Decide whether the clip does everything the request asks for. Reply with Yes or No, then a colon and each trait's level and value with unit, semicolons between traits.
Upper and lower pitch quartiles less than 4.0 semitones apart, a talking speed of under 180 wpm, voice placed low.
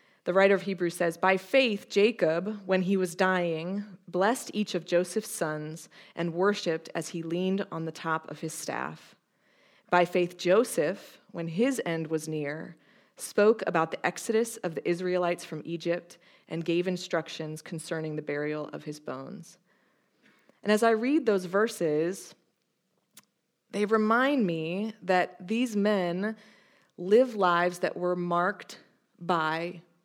No: average, 3.6 semitones; average, 145 wpm; medium, 180 Hz